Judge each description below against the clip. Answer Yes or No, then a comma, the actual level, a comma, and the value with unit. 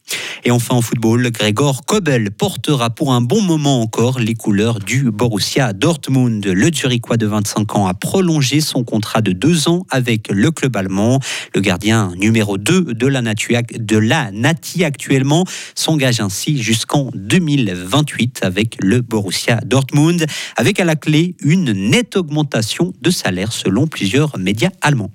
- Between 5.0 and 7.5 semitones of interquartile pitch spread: Yes, wide, 5.5 semitones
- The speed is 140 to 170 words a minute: Yes, average, 155 wpm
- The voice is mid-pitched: No, low, 125 Hz